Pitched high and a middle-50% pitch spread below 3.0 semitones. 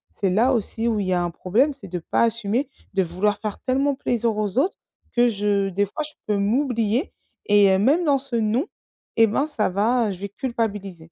No: high, 215 Hz; average, 4.0 semitones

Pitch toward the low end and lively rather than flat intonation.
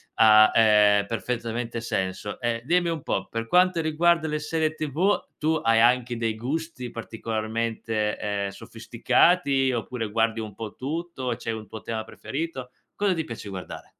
Yes: low, 115 Hz; wide, 5.9 semitones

